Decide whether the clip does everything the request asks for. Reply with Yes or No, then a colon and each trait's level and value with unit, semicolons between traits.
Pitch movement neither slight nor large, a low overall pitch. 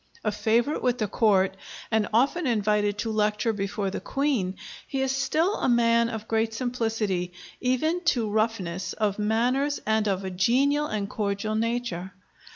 No: average, 3.3 semitones; high, 220 Hz